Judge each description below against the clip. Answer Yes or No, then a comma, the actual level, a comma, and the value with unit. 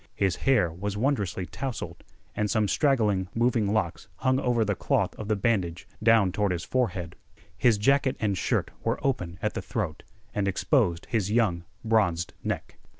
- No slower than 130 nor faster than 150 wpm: No, average, 165 wpm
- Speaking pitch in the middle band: No, low, 105 Hz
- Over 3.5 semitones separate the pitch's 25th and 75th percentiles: Yes, average, 4.1 semitones